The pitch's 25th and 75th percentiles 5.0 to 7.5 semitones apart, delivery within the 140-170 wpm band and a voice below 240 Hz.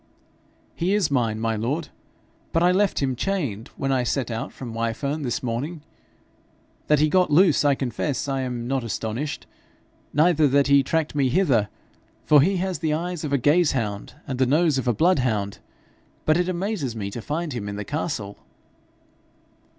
No: wide, 5.4 semitones; average, 180 wpm; medium, 140 Hz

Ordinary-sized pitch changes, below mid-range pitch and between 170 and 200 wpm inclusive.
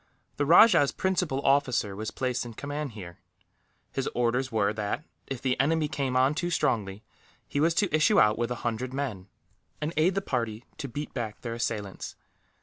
Yes: average, 4.8 semitones; low, 130 Hz; average, 180 wpm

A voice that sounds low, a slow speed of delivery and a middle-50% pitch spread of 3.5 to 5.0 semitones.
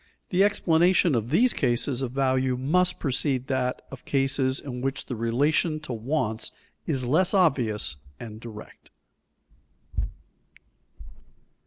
Yes: low, 130 Hz; slow, 120 wpm; average, 4.3 semitones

